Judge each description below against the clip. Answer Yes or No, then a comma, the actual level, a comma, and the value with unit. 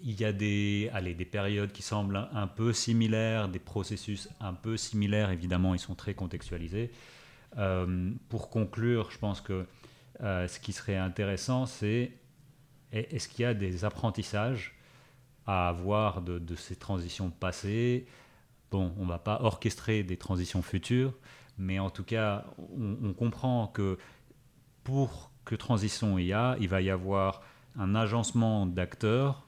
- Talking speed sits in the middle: Yes, average, 155 wpm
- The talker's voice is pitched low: Yes, low, 105 Hz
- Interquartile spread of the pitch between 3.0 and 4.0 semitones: Yes, average, 3.7 semitones